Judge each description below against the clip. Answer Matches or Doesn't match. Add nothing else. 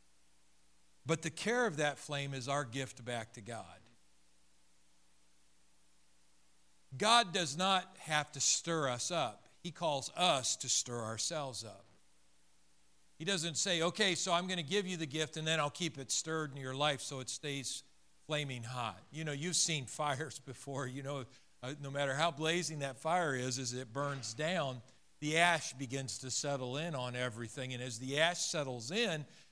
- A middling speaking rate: Matches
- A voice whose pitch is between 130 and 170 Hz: Matches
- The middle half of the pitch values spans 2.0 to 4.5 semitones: Doesn't match